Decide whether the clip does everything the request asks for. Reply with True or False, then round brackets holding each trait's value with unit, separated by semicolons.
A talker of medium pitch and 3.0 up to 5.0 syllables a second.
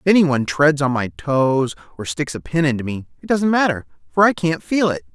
False (145 Hz; 5.5 syllables/s)